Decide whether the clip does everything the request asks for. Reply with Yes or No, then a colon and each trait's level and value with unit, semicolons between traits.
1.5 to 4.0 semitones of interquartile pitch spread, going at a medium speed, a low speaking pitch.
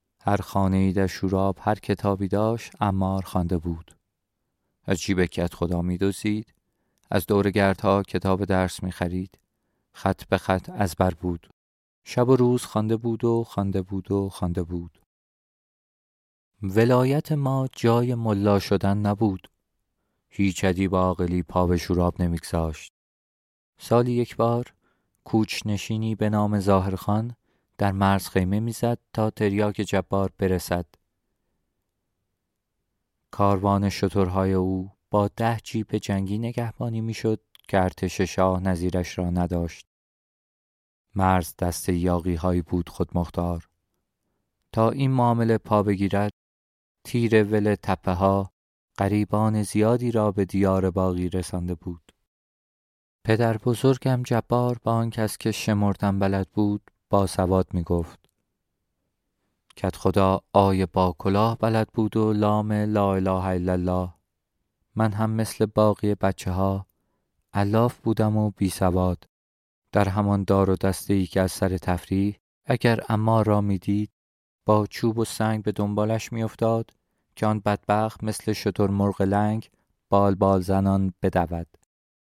Yes: average, 2.8 semitones; average, 130 wpm; low, 100 Hz